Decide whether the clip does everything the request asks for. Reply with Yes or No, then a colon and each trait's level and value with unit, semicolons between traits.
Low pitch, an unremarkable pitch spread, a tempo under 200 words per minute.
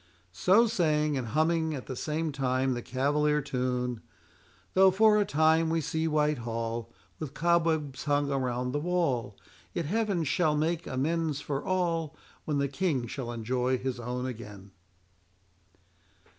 No: medium, 145 Hz; average, 4.4 semitones; average, 145 wpm